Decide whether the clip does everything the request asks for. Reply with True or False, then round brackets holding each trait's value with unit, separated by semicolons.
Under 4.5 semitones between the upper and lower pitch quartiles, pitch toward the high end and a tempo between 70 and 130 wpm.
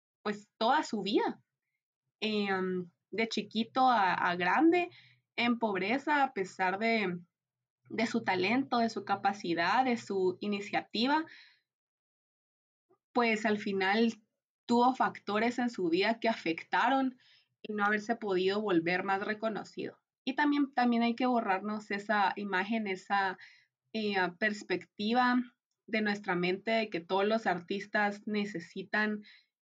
True (3.8 semitones; 210 Hz; 125 wpm)